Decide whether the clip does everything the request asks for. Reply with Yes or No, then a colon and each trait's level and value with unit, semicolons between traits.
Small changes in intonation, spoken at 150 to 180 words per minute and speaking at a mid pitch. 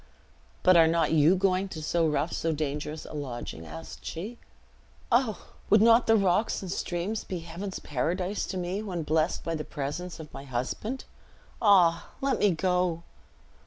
No: average, 4.0 semitones; average, 160 wpm; medium, 175 Hz